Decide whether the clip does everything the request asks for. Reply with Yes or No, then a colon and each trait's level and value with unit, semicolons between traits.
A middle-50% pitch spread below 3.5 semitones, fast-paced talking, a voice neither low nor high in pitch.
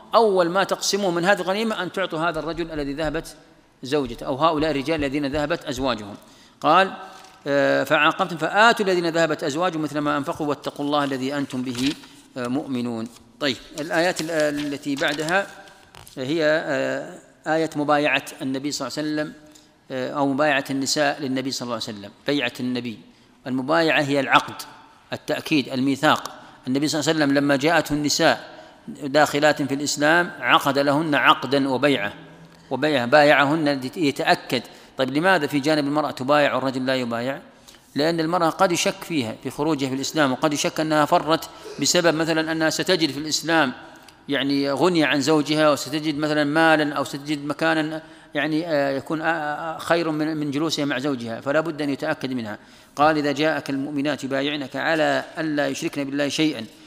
Yes: narrow, 2.4 semitones; fast, 145 wpm; medium, 150 Hz